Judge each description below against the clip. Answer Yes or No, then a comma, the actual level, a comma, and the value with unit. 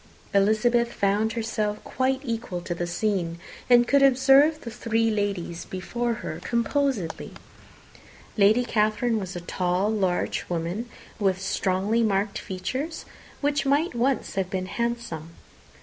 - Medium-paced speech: No, slow, 130 wpm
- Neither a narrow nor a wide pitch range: Yes, average, 4.2 semitones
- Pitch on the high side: Yes, high, 215 Hz